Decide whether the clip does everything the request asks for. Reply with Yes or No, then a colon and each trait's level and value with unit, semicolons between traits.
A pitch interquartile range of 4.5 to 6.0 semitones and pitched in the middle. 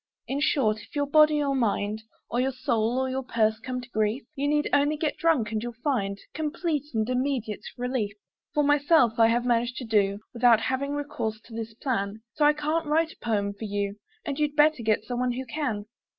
No: average, 4.9 semitones; very high, 250 Hz